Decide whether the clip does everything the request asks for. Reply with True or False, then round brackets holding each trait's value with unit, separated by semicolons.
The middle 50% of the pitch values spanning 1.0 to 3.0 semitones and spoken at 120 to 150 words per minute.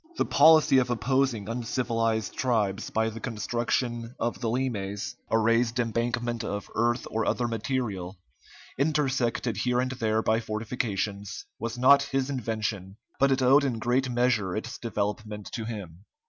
True (2.6 semitones; 145 wpm)